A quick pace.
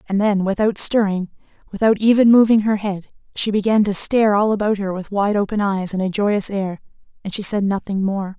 Yes: fast, 210 wpm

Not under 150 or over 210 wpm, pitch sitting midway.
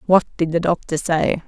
Yes: fast, 205 wpm; medium, 170 Hz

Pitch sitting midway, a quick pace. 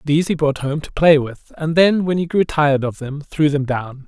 Yes: medium, 150 Hz; fast, 265 wpm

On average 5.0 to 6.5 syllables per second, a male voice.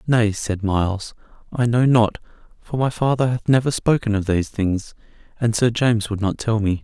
Yes: 5.2 syllables/s; male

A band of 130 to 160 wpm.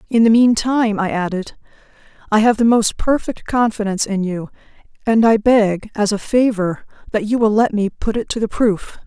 No: average, 200 wpm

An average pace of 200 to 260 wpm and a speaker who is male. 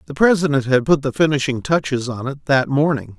Yes: fast, 205 wpm; male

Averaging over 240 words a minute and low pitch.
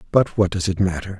Yes: fast, 250 wpm; very low, 95 Hz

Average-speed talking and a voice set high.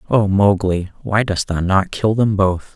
No: average, 195 wpm; low, 100 Hz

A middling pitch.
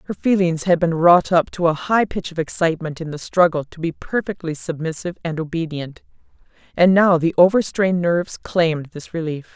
Yes: medium, 170 Hz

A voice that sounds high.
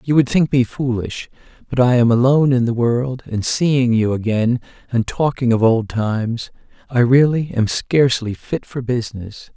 No: low, 125 Hz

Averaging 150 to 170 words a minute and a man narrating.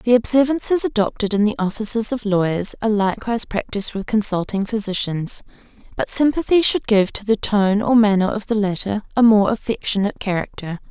No: average, 165 wpm; female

